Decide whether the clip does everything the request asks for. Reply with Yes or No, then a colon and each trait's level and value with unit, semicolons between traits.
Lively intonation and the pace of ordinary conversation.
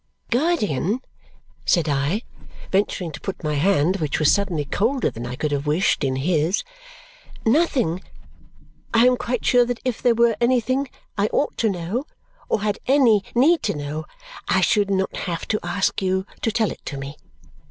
Yes: wide, 7.3 semitones; average, 175 wpm